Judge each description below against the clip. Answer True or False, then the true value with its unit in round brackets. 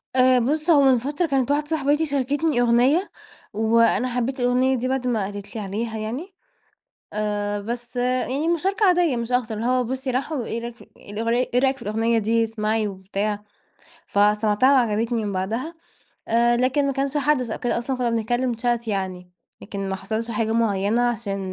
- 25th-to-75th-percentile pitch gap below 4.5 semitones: True (3.4 semitones)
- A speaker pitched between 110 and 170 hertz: False (240 Hz)